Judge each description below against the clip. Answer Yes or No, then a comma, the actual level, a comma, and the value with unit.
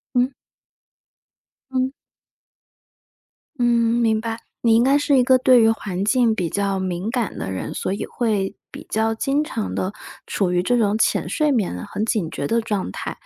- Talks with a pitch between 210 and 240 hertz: Yes, high, 225 Hz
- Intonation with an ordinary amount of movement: Yes, average, 3.8 semitones